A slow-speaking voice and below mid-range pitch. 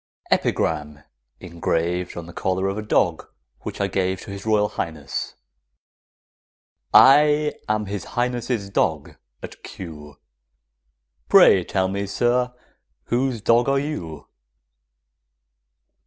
Yes: slow, 110 wpm; low, 100 Hz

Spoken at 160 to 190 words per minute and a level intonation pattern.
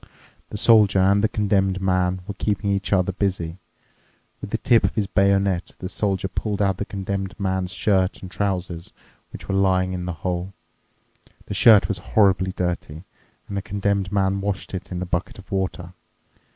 Yes: average, 180 wpm; narrow, 1.4 semitones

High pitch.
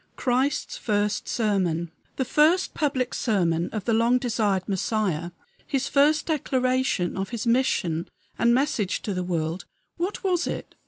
Yes: high, 230 Hz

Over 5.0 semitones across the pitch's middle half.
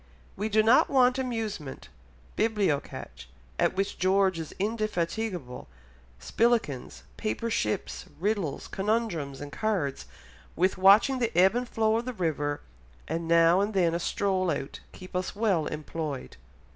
Yes: wide, 5.4 semitones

